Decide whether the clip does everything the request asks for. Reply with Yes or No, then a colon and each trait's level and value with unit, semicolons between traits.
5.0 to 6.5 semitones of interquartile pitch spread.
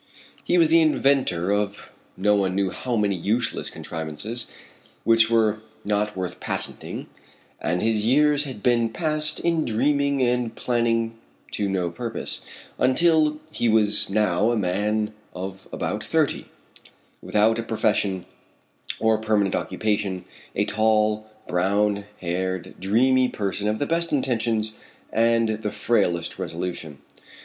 No: average, 3.4 semitones